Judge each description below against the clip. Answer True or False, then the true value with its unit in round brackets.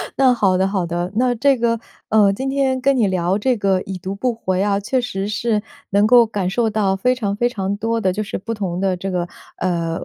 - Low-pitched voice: False (205 Hz)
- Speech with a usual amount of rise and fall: True (3.9 semitones)